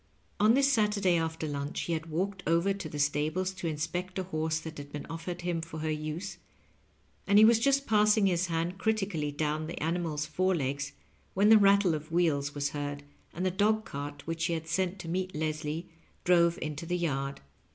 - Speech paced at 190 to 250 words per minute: Yes, average, 200 wpm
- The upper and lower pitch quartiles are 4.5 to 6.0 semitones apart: No, average, 3.7 semitones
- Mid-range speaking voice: Yes, medium, 165 Hz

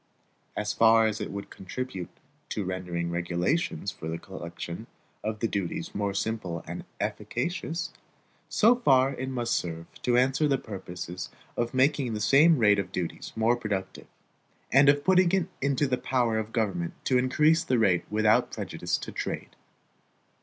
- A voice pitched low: Yes, low, 110 Hz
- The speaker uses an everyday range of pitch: No, wide, 5.9 semitones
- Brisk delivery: No, average, 160 wpm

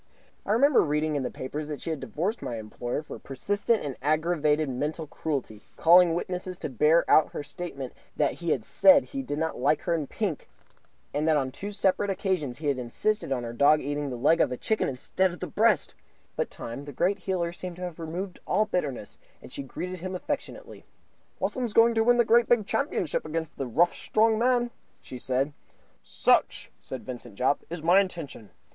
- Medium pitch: Yes, medium, 160 Hz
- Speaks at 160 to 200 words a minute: Yes, average, 195 wpm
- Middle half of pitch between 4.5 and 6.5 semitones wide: Yes, wide, 5.4 semitones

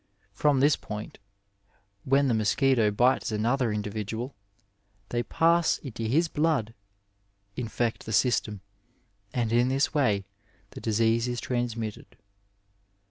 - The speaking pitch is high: No, low, 120 Hz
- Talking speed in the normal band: No, slow, 120 wpm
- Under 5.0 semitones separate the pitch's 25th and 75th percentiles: Yes, average, 3.6 semitones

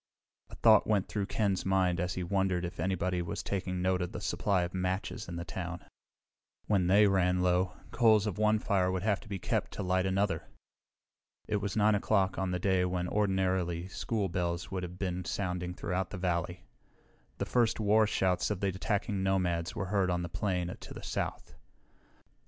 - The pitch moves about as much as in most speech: No, narrow, 1.9 semitones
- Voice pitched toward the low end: Yes, very low, 95 Hz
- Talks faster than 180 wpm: Yes, average, 190 wpm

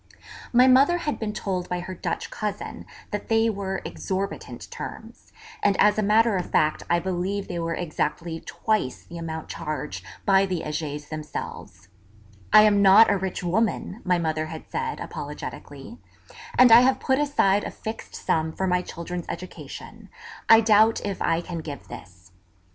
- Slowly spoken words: No, average, 165 wpm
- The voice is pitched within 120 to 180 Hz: No, high, 190 Hz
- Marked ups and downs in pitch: No, average, 4.4 semitones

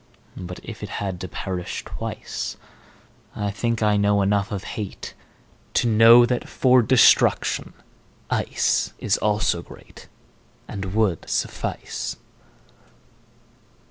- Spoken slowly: Yes, slow, 95 wpm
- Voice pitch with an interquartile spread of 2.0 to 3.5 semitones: Yes, average, 2.8 semitones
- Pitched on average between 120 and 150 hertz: No, low, 105 Hz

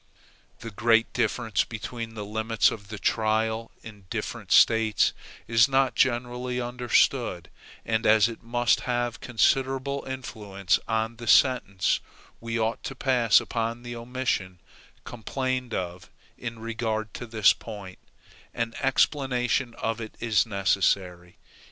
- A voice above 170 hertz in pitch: No, low, 115 Hz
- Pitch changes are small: Yes, narrow, 2.1 semitones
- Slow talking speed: Yes, slow, 130 wpm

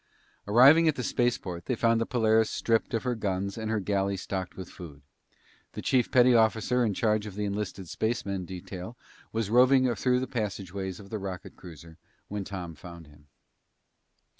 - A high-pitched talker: No, low, 105 Hz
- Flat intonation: No, average, 3.9 semitones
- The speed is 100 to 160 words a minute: No, average, 175 wpm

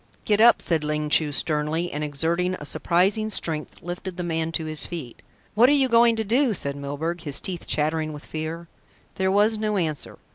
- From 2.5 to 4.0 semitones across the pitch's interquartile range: No, average, 5.0 semitones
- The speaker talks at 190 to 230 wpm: Yes, average, 195 wpm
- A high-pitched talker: No, medium, 170 Hz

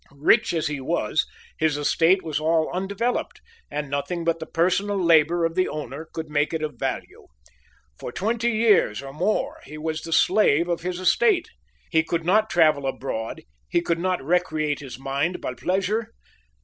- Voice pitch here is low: No, medium, 165 Hz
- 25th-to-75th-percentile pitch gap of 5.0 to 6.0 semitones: No, average, 3.6 semitones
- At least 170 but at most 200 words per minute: Yes, average, 175 wpm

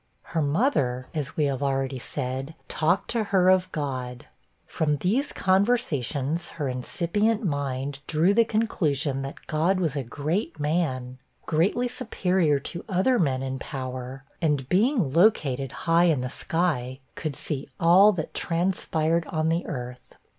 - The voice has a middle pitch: Yes, medium, 155 Hz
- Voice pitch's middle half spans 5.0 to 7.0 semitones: Yes, average, 5.3 semitones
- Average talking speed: Yes, average, 145 wpm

